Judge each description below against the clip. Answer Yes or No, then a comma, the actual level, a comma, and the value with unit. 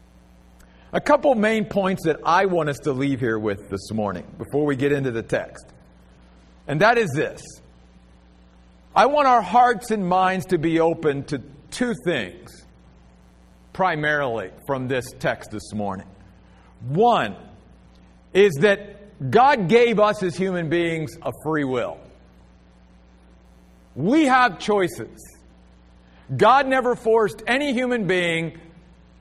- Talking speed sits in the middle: No, slow, 130 wpm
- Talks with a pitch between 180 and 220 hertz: No, low, 135 Hz